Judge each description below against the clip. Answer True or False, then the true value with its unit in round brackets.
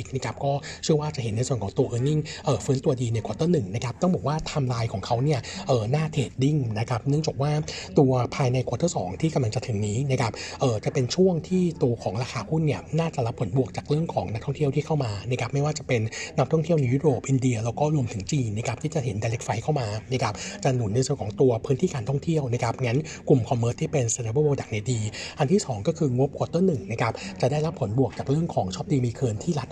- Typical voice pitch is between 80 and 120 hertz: False (135 Hz)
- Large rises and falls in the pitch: False (4.0 semitones)